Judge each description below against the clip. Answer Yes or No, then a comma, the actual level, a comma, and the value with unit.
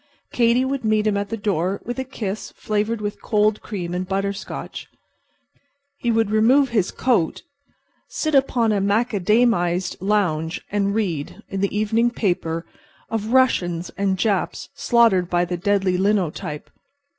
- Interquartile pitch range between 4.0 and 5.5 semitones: No, average, 3.6 semitones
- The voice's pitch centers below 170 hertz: No, high, 205 Hz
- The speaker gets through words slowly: No, average, 145 wpm